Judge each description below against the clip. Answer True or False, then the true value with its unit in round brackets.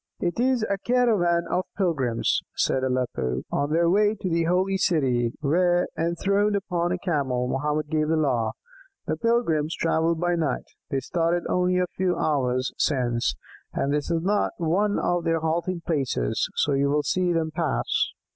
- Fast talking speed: False (165 wpm)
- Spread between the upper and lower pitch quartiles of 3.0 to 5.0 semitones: True (4.3 semitones)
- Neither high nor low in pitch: True (165 Hz)